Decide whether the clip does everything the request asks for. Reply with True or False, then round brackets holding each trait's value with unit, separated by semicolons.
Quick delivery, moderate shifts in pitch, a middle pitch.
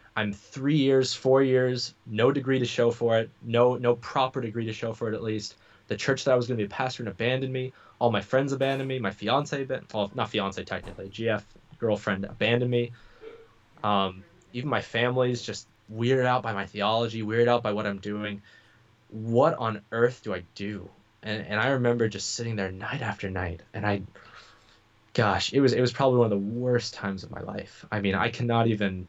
False (210 wpm; 3.3 semitones; 115 Hz)